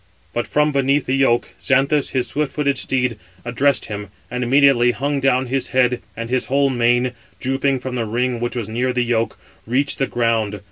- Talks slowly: No, average, 190 wpm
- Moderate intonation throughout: No, narrow, 2.2 semitones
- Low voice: Yes, low, 125 Hz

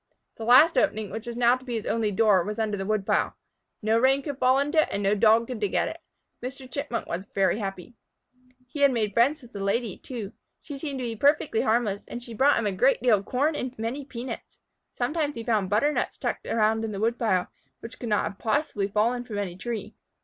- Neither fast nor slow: No, fast, 225 wpm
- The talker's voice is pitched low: No, high, 230 Hz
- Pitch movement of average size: Yes, average, 3.6 semitones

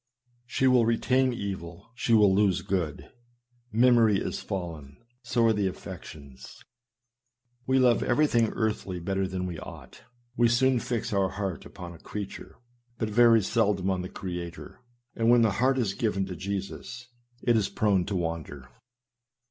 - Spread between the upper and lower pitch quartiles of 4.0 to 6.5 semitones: Yes, average, 4.4 semitones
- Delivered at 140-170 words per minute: Yes, average, 155 wpm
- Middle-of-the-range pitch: No, low, 100 Hz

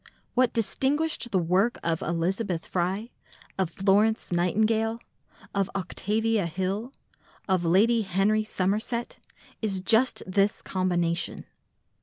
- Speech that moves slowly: Yes, slow, 105 wpm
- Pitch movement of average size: Yes, average, 3.4 semitones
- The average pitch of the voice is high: Yes, high, 195 Hz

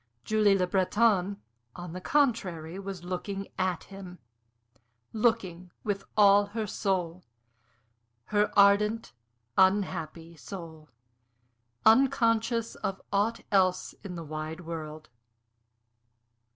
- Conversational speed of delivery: No, slow, 100 wpm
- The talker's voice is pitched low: No, high, 195 Hz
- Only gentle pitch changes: No, average, 3.1 semitones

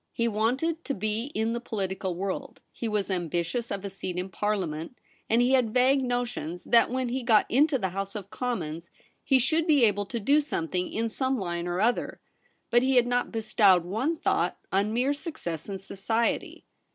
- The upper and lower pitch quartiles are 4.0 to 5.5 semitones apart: Yes, average, 4.7 semitones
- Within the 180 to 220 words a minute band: Yes, average, 190 wpm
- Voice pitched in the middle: No, high, 225 Hz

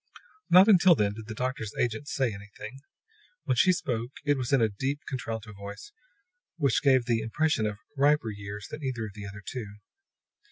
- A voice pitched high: No, low, 120 Hz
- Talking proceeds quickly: No, average, 185 wpm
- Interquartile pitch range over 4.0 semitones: Yes, average, 5.0 semitones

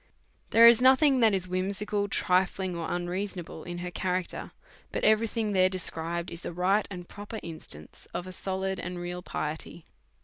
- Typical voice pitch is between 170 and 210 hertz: Yes, medium, 185 Hz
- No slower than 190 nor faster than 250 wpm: No, average, 180 wpm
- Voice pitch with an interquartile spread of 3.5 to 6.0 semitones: No, narrow, 2.6 semitones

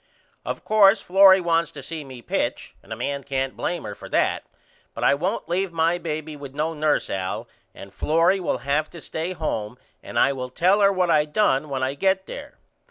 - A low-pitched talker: No, medium, 155 Hz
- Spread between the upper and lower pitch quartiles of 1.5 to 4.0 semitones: No, average, 4.8 semitones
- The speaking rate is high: Yes, fast, 210 wpm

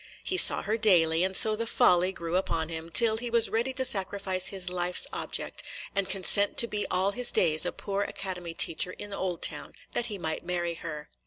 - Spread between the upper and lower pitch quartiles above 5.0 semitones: No, average, 3.4 semitones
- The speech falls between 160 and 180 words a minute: No, average, 200 wpm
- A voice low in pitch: No, high, 190 Hz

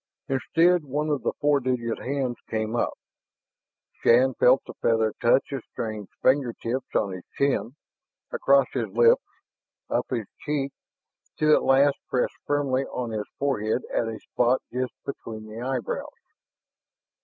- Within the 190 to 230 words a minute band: No, average, 145 wpm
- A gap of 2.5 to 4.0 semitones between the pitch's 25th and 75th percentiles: Yes, average, 3.4 semitones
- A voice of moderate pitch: No, low, 125 Hz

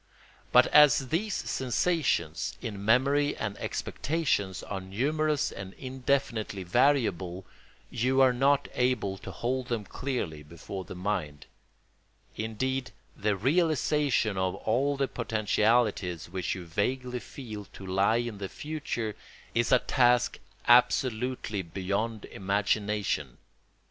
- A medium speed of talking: No, slow, 115 wpm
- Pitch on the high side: No, low, 115 Hz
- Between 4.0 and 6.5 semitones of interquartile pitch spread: Yes, average, 5.1 semitones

